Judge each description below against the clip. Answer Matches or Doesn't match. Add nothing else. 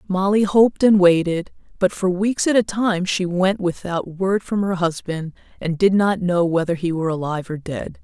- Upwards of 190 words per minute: Matches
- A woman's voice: Matches